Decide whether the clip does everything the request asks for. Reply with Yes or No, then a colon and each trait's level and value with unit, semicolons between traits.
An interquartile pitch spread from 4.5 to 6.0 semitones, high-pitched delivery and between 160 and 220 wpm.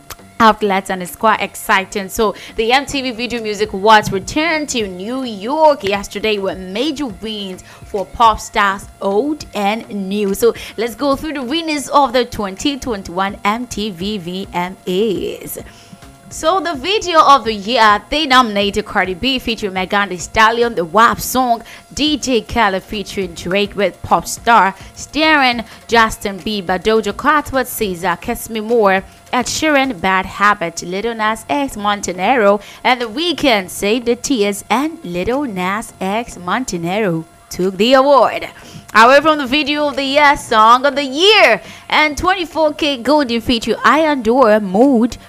No: wide, 5.4 semitones; high, 225 Hz; average, 145 wpm